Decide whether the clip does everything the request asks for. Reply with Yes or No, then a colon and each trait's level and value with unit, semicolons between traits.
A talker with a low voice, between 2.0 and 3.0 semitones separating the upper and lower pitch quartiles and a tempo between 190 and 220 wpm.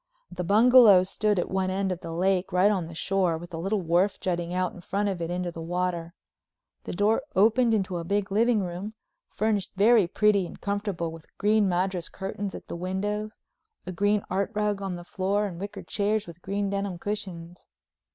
No: high, 190 Hz; narrow, 2.6 semitones; average, 200 wpm